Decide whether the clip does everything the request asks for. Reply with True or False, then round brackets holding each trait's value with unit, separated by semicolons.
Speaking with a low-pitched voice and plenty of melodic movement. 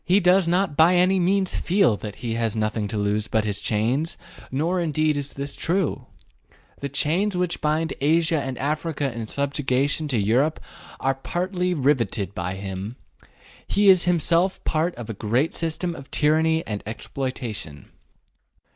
False (145 Hz; 6.9 semitones)